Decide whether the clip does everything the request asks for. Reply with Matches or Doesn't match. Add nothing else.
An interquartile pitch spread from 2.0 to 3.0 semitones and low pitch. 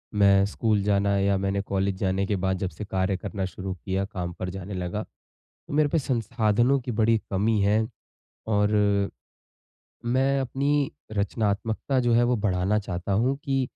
Doesn't match